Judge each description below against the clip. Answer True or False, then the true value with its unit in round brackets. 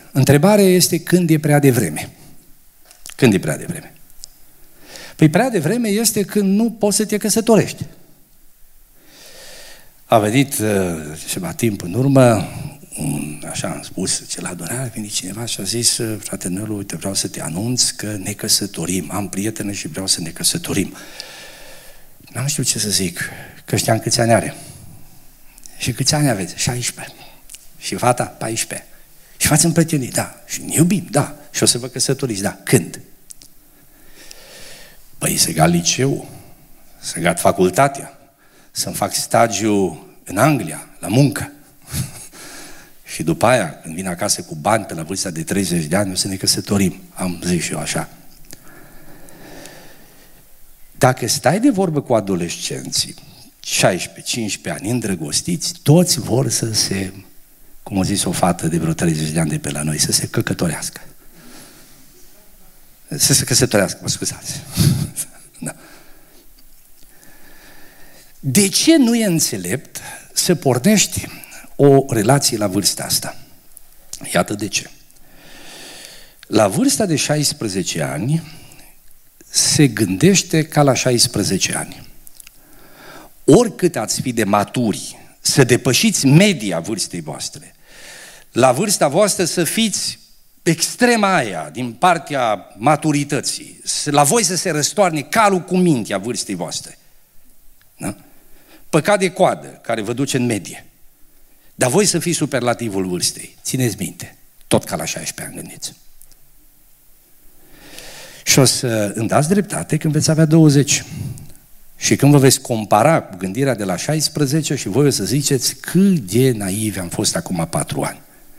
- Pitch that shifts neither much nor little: False (7.2 semitones)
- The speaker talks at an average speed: True (140 wpm)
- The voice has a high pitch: False (135 Hz)